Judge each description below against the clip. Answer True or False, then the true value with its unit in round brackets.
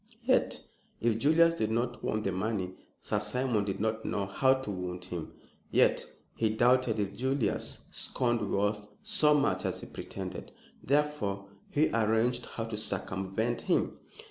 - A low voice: True (110 Hz)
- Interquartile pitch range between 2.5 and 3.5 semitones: False (4.2 semitones)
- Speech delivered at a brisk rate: False (150 wpm)